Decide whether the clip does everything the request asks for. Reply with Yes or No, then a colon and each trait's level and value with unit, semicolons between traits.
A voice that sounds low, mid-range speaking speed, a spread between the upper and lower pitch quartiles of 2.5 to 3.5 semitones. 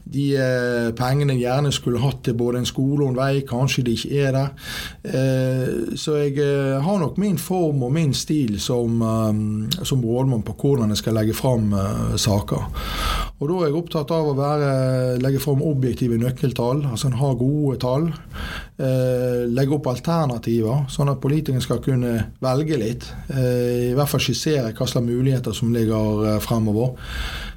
Yes: low, 130 Hz; average, 160 wpm; average, 2.9 semitones